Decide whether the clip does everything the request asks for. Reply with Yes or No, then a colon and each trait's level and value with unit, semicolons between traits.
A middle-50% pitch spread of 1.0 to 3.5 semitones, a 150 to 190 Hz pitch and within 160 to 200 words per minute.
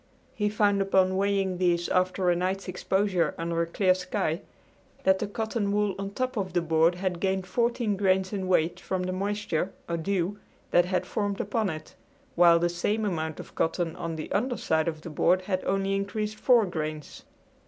Yes: average, 2.7 semitones; medium, 185 Hz; average, 190 wpm